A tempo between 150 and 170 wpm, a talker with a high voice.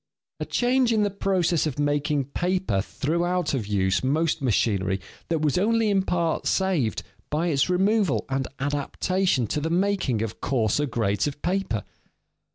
No: average, 160 wpm; medium, 155 Hz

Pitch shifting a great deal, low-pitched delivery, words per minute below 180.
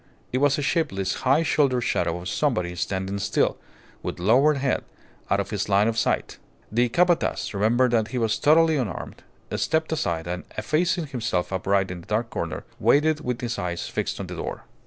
No: wide, 6.9 semitones; low, 120 Hz; average, 185 wpm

